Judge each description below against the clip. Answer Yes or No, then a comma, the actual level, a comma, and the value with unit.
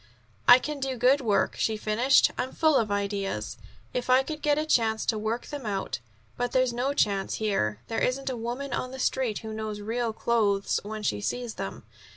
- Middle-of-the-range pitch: No, high, 235 Hz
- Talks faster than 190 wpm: Yes, average, 200 wpm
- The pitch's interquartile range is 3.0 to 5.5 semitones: Yes, average, 3.5 semitones